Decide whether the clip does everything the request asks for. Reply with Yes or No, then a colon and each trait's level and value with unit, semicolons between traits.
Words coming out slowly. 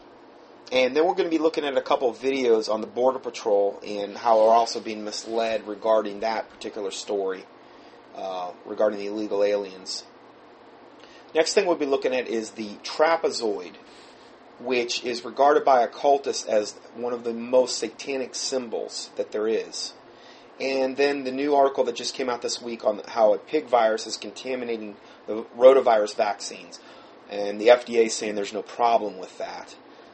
No: average, 170 wpm